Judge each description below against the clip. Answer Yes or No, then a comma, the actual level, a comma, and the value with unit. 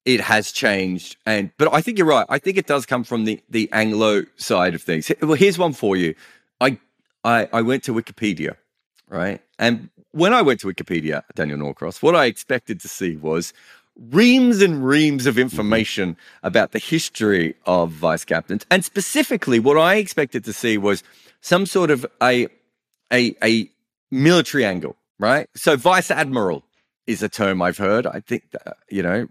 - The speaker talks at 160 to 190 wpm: Yes, average, 180 wpm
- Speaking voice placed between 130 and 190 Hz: No, low, 120 Hz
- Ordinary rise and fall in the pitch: No, wide, 7.5 semitones